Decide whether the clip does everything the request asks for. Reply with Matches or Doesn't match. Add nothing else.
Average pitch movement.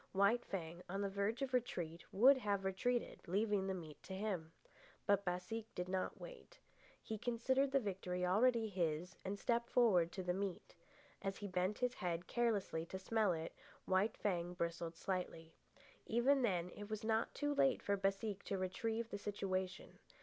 Matches